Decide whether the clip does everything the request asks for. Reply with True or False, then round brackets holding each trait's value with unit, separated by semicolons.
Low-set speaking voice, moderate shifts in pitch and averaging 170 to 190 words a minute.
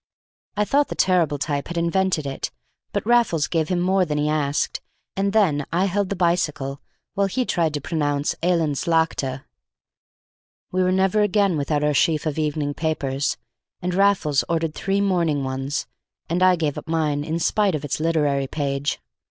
False (160 Hz; 4.1 semitones; 175 wpm)